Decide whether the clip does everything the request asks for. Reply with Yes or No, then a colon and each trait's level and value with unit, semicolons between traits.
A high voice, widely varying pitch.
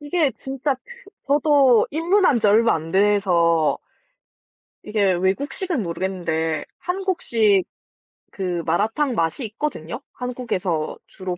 Yes: high, 210 Hz; wide, 7.9 semitones